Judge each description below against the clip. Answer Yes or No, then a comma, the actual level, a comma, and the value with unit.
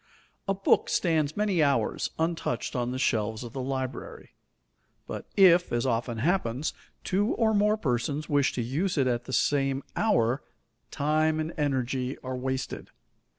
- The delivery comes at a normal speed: Yes, average, 150 wpm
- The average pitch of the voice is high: No, medium, 140 Hz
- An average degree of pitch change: Yes, average, 4.9 semitones